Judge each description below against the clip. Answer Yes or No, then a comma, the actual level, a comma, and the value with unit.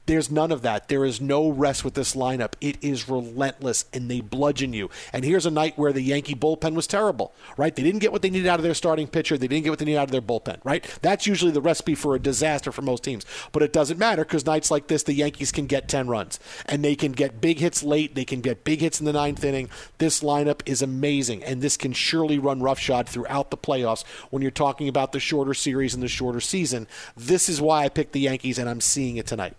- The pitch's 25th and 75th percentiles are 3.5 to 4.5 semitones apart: No, average, 2.8 semitones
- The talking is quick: Yes, fast, 260 wpm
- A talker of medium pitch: Yes, medium, 145 Hz